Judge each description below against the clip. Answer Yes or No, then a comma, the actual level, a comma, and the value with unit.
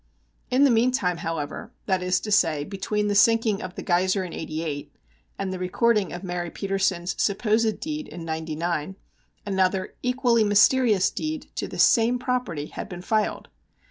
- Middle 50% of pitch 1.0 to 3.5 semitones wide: No, average, 4.4 semitones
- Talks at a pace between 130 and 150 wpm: No, average, 160 wpm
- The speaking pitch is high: Yes, high, 195 Hz